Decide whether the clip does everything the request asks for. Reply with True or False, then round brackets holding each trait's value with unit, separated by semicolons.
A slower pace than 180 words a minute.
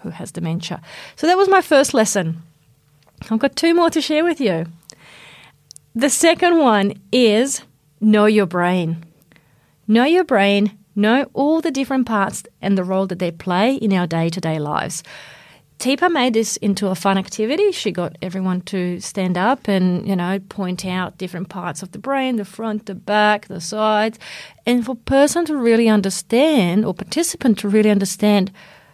True (170 wpm)